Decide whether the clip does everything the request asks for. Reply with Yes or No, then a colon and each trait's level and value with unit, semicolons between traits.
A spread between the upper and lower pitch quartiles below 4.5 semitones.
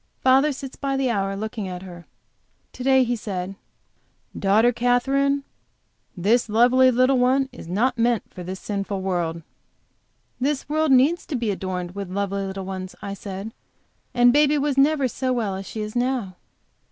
No: average, 5.2 semitones